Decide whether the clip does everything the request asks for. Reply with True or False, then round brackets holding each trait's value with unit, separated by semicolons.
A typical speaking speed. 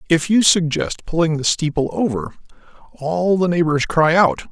True (160 wpm)